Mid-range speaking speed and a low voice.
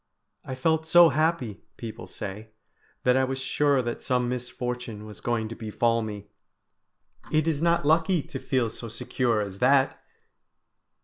Yes: average, 150 wpm; low, 125 Hz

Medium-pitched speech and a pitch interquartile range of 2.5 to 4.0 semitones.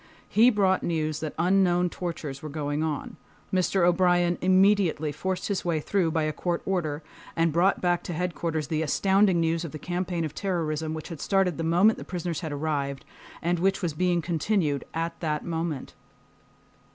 Yes: medium, 170 Hz; average, 2.8 semitones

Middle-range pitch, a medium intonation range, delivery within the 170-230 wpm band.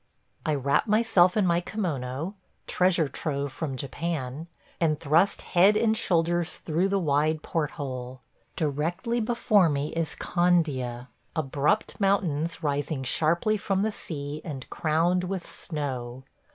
No: medium, 160 Hz; average, 4.2 semitones; average, 140 wpm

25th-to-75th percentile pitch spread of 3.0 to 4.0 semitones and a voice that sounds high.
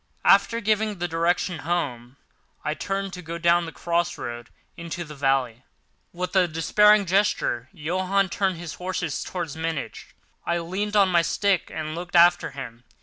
No: average, 3.3 semitones; medium, 170 Hz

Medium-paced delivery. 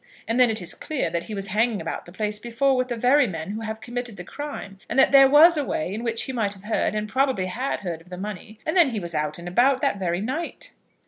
No: fast, 275 wpm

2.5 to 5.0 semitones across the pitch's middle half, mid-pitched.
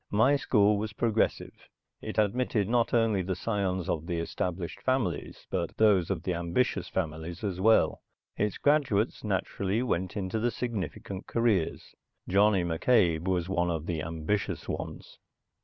No: average, 4.2 semitones; low, 100 Hz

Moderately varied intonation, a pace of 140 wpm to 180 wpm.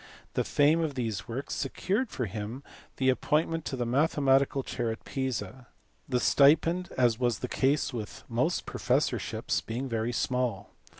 Yes: average, 3.2 semitones; average, 155 wpm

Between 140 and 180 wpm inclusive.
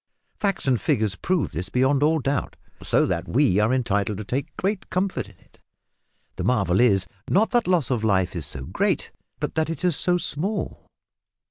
No: average, 190 wpm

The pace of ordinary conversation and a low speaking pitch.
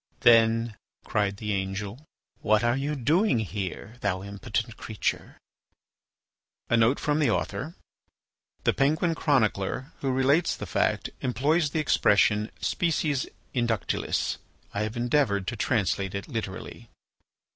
No: slow, 105 wpm; low, 115 Hz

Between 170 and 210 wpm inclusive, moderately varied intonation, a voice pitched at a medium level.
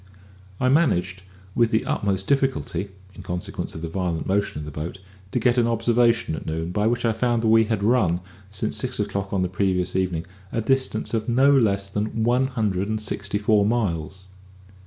No: average, 195 wpm; average, 4.0 semitones; low, 105 Hz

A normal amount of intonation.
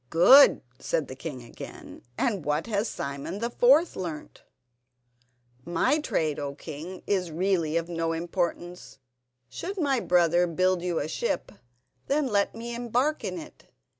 No: wide, 6.3 semitones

